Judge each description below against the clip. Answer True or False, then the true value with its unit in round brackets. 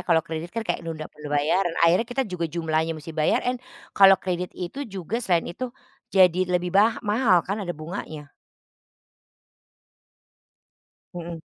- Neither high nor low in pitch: True (175 Hz)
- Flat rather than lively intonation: False (3.4 semitones)